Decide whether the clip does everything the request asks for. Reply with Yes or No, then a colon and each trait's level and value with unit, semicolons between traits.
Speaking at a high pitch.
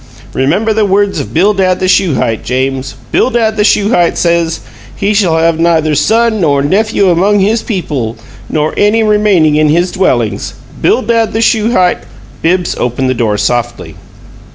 No: medium, 180 Hz